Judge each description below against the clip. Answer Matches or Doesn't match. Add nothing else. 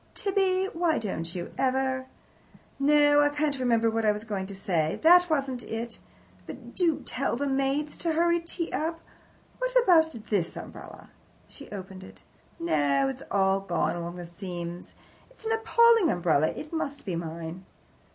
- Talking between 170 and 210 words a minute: Doesn't match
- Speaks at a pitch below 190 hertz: Doesn't match